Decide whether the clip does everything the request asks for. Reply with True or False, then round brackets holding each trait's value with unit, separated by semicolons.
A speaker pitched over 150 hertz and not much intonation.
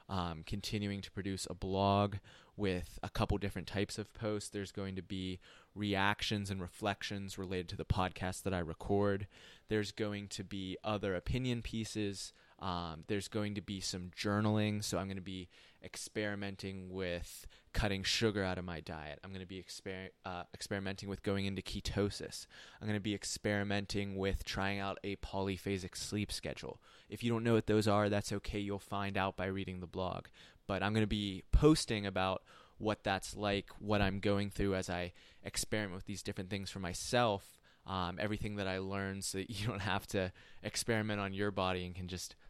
False (100 Hz; 1.8 semitones)